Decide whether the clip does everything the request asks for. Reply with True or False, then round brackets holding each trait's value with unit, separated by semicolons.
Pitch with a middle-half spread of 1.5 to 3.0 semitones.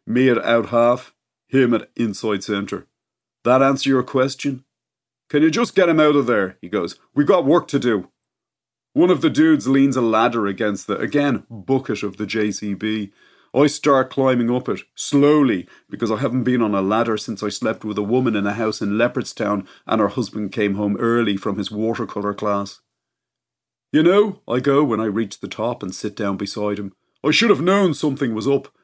False (4.7 semitones)